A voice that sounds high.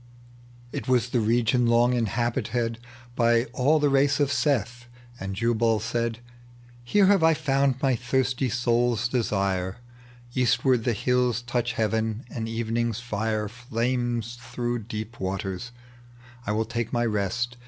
No: low, 120 Hz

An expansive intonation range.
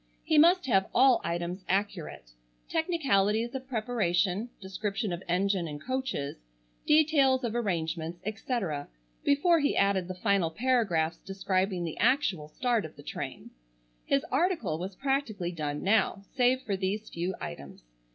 Yes: wide, 6.6 semitones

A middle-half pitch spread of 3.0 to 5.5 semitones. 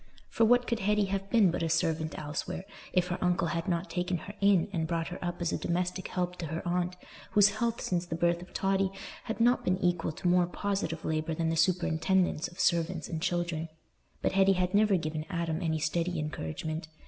No: narrow, 2.5 semitones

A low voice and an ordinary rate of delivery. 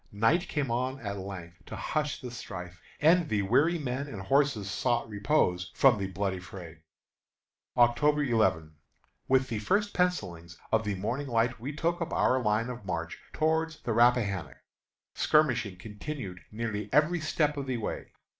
Yes: low, 120 Hz; average, 160 wpm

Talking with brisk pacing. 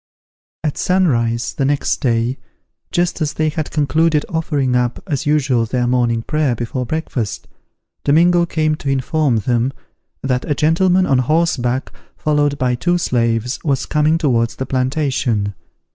No: average, 145 wpm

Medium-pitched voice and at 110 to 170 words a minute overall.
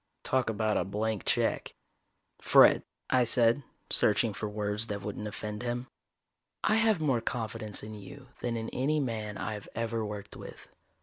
No: low, 110 Hz; average, 160 wpm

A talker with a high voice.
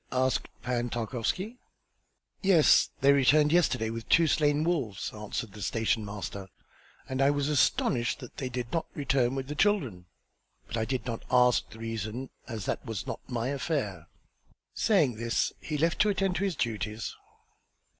No: low, 125 Hz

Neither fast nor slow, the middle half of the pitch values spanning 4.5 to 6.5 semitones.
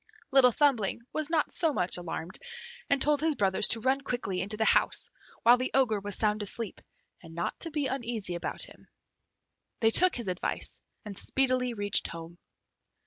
Yes: average, 175 wpm; wide, 5.5 semitones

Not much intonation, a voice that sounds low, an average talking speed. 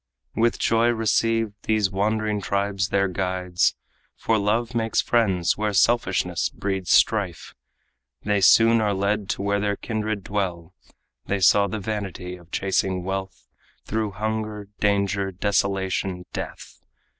No: narrow, 2.2 semitones; low, 100 Hz; slow, 130 wpm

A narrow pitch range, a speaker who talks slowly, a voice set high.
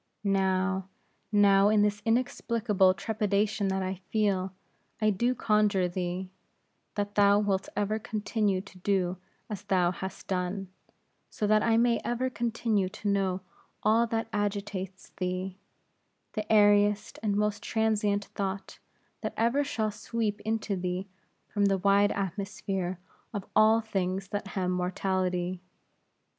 Yes: narrow, 2.1 semitones; slow, 130 wpm; high, 200 Hz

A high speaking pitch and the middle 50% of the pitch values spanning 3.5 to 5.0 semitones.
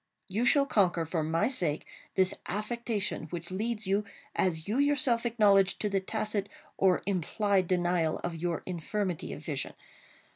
Yes: high, 195 Hz; average, 3.8 semitones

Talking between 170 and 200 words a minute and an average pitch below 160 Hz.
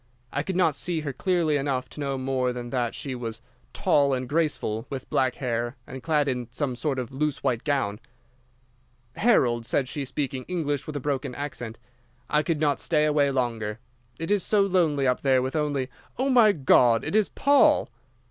Yes: average, 185 wpm; medium, 140 Hz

